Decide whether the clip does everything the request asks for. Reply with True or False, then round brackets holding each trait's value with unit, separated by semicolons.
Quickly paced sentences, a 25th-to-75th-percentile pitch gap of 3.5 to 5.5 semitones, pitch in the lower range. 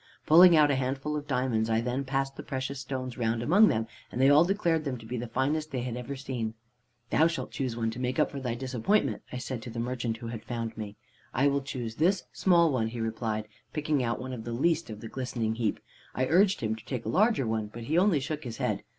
True (250 wpm; 4.2 semitones; 130 Hz)